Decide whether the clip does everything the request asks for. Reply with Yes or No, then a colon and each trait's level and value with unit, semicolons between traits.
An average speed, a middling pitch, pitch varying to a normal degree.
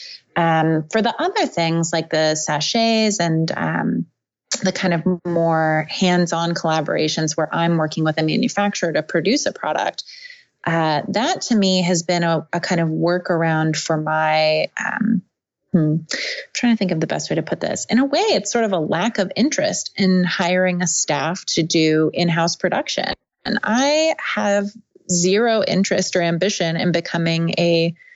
Yes: average, 170 wpm; medium, 175 Hz; average, 4.1 semitones